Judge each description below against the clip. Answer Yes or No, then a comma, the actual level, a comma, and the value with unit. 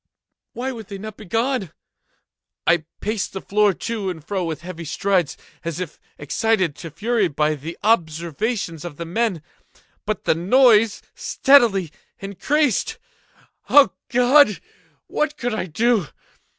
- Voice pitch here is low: No, high, 200 Hz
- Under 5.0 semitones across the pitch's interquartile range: No, wide, 5.6 semitones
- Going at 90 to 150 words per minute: Yes, slow, 135 wpm